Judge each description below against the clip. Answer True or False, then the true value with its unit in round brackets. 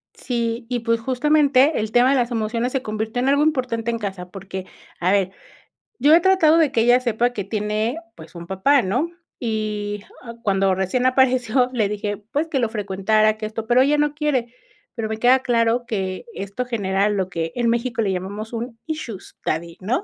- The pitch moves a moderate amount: True (3.7 semitones)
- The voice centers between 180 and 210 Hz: False (230 Hz)